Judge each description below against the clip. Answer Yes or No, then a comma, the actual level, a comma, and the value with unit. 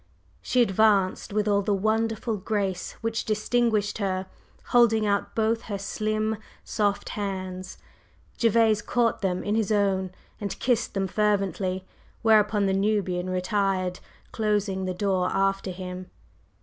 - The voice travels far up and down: No, narrow, 2.4 semitones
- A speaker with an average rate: No, slow, 130 wpm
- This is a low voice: No, high, 205 Hz